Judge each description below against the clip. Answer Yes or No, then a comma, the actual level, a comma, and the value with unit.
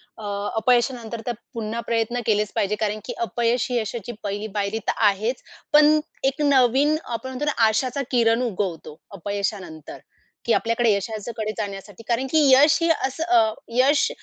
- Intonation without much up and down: No, average, 3.4 semitones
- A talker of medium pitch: No, high, 230 Hz